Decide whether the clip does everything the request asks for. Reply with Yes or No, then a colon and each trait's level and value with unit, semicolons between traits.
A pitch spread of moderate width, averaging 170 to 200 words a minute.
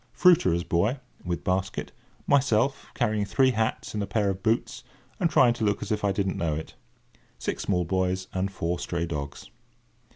Yes: average, 3.9 semitones; average, 175 wpm